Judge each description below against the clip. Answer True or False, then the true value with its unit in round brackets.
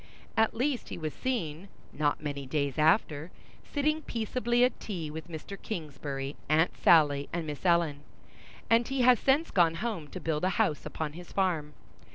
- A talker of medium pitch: True (165 Hz)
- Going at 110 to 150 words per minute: False (170 wpm)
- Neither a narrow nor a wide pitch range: False (6.9 semitones)